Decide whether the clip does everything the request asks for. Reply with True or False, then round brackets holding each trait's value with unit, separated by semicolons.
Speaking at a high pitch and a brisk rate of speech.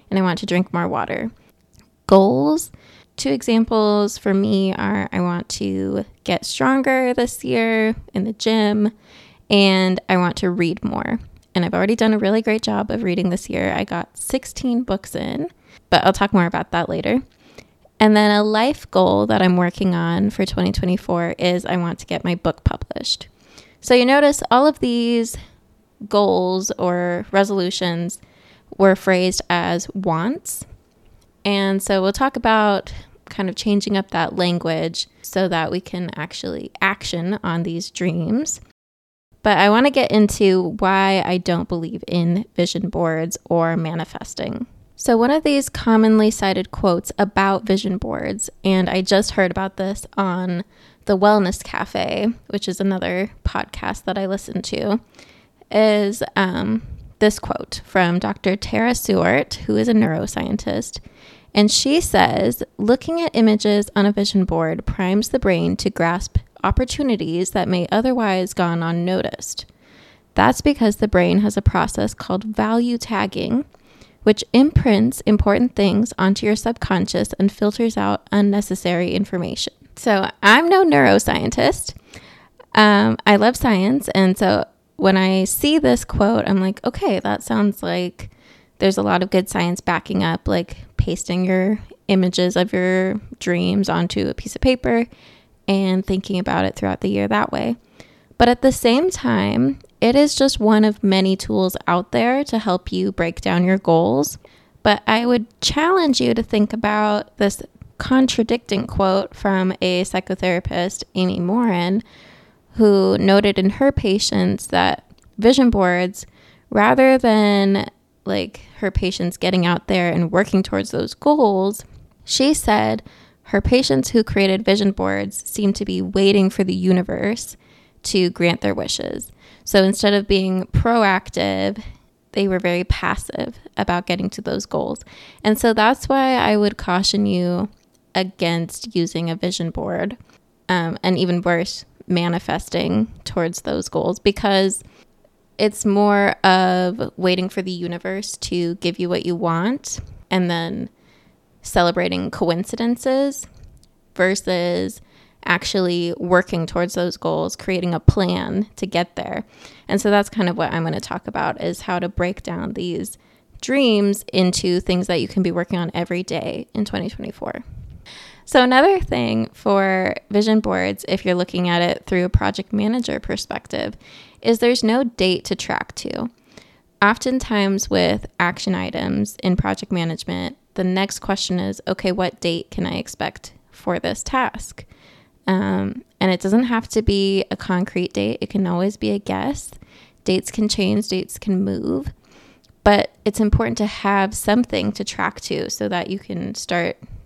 False (195 Hz; 155 wpm)